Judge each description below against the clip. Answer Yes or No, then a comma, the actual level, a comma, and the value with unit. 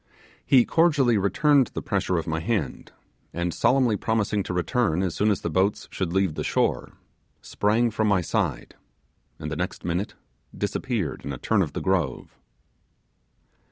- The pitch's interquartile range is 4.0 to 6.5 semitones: Yes, average, 4.8 semitones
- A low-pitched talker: Yes, low, 100 Hz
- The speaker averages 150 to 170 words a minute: Yes, average, 160 wpm